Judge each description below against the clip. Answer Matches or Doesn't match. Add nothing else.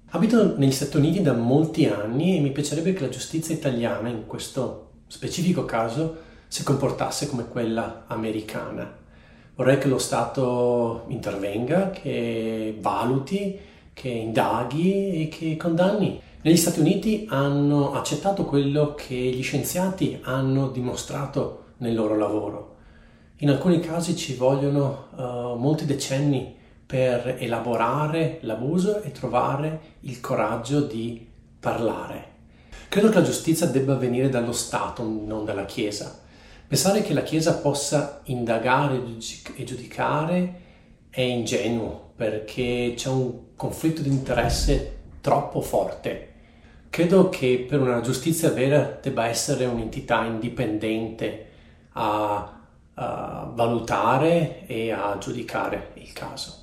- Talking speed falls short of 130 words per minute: Matches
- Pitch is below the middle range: Matches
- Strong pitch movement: Doesn't match